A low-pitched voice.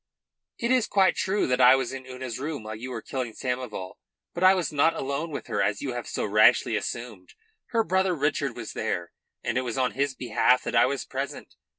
Yes: low, 130 Hz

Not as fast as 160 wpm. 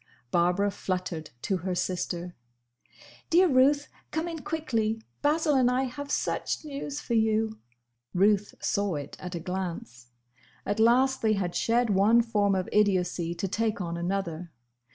Yes: average, 150 wpm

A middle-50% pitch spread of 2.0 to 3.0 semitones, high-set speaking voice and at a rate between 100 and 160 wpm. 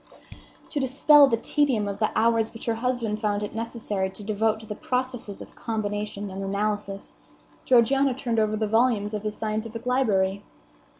No: average, 2.7 semitones; high, 220 Hz; average, 170 wpm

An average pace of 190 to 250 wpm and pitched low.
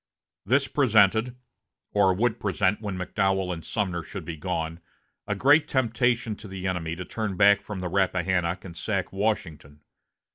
No: average, 155 wpm; very low, 95 Hz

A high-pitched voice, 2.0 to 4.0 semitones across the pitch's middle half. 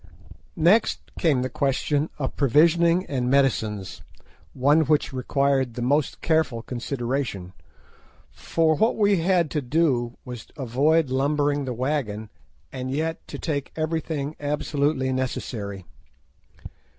No: medium, 140 Hz; average, 3.7 semitones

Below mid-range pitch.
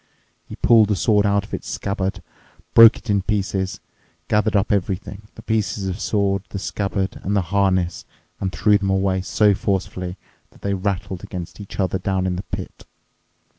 Yes: low, 100 Hz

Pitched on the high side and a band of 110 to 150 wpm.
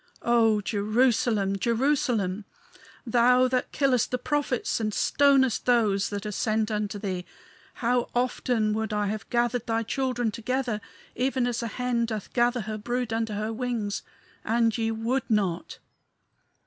Yes: high, 230 Hz; average, 145 wpm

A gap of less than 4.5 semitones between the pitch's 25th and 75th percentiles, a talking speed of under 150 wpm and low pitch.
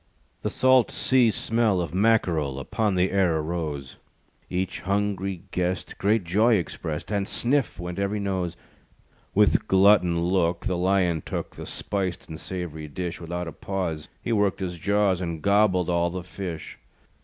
No: average, 2.9 semitones; average, 155 wpm; very low, 90 Hz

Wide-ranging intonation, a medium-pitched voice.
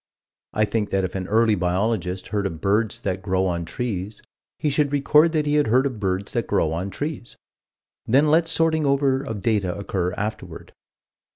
No: wide, 6.6 semitones; low, 110 Hz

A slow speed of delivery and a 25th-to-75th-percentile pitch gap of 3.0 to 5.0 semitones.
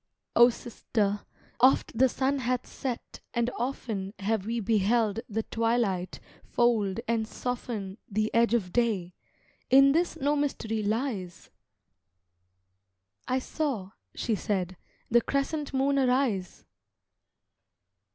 Yes: slow, 110 wpm; average, 3.8 semitones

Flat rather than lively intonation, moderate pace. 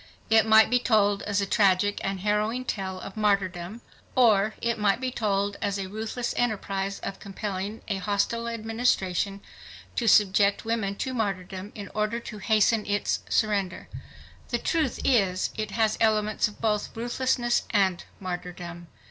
Yes: narrow, 2.3 semitones; average, 150 wpm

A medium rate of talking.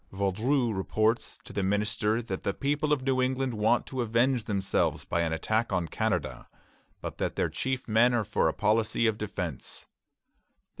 Yes: average, 170 wpm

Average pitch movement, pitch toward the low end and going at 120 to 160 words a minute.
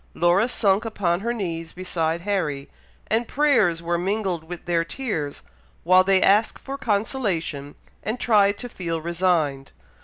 No: average, 4.3 semitones; medium, 185 Hz; average, 145 wpm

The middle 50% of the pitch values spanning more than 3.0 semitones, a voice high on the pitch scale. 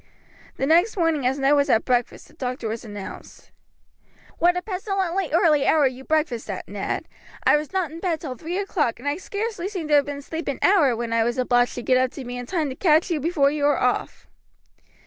Yes: average, 5.2 semitones; very high, 290 Hz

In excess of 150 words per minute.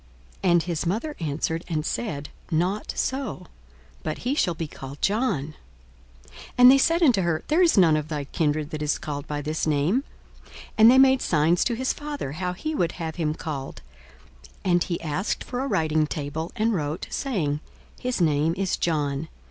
Yes: average, 190 wpm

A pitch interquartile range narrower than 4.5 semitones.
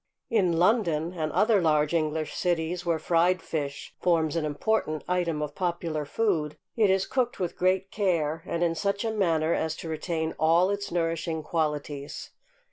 Yes: average, 2.8 semitones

